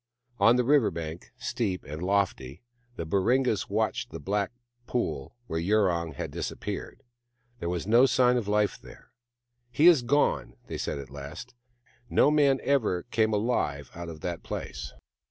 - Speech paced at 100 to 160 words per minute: No, average, 170 wpm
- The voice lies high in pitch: No, low, 105 Hz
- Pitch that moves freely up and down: Yes, wide, 6.6 semitones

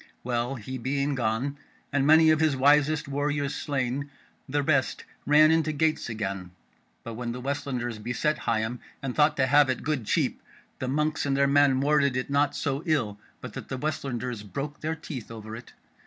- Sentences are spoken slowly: No, average, 185 wpm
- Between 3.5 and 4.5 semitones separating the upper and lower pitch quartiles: No, average, 3.1 semitones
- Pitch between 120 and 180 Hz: Yes, medium, 140 Hz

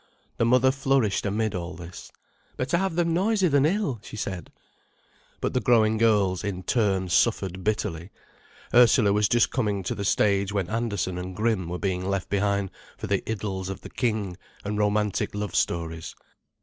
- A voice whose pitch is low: Yes, low, 105 Hz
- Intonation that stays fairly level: No, average, 3.8 semitones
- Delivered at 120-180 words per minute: Yes, average, 170 wpm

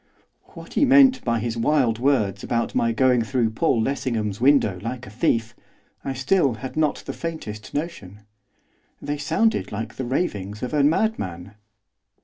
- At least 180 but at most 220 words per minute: No, average, 155 wpm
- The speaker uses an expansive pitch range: No, average, 4.9 semitones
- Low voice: Yes, low, 125 Hz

